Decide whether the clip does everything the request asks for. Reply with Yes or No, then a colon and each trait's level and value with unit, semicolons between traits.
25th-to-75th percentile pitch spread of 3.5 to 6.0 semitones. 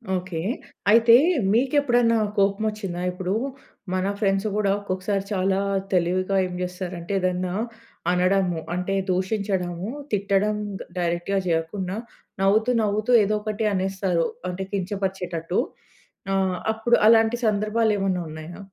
No: average, 2.7 semitones